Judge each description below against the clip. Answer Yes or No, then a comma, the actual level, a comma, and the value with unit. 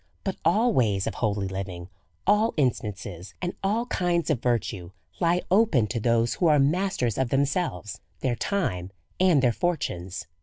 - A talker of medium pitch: No, low, 130 Hz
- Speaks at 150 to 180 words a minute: Yes, average, 155 wpm